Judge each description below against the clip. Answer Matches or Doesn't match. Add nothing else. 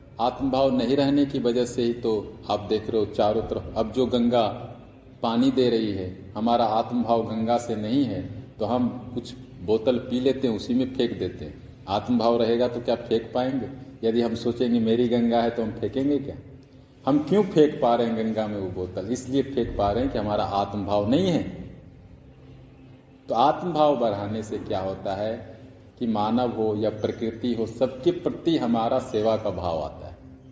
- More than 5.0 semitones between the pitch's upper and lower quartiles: Doesn't match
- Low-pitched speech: Matches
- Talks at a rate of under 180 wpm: Doesn't match